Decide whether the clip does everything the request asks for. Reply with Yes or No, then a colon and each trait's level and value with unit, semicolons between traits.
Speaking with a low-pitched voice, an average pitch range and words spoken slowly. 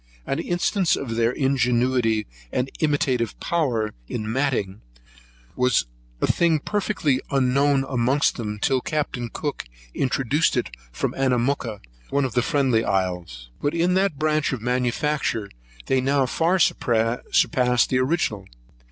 Yes: low, 130 Hz; average, 3.7 semitones; slow, 130 wpm